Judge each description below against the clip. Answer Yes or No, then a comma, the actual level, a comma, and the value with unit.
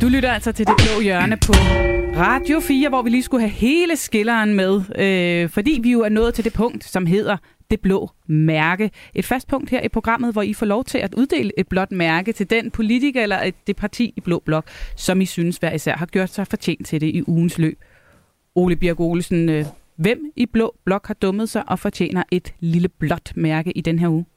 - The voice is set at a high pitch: Yes, high, 195 Hz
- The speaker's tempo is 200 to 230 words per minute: Yes, fast, 225 wpm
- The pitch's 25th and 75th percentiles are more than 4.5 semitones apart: Yes, average, 5.0 semitones